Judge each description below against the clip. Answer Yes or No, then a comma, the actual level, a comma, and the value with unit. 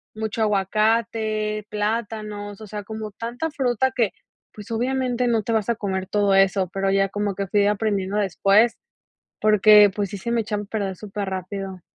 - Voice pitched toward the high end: Yes, high, 210 Hz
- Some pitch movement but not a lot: No, narrow, 2.1 semitones